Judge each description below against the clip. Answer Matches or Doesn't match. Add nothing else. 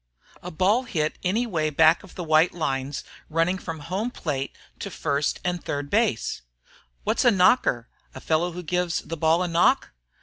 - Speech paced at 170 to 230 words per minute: Matches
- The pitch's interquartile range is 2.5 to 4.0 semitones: Matches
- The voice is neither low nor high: Matches